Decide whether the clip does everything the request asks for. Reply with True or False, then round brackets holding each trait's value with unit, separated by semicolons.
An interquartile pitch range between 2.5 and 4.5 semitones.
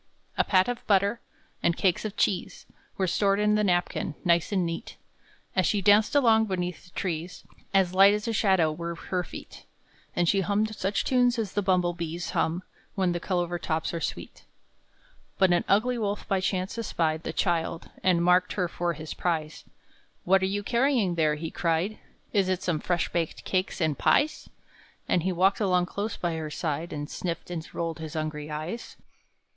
True (3.1 semitones)